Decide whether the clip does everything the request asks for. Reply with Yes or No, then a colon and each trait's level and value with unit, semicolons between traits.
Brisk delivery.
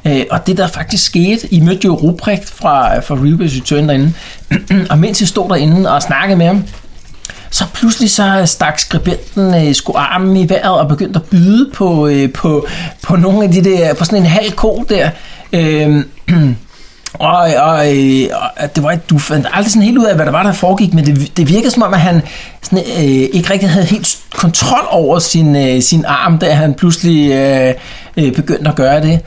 No: average, 185 wpm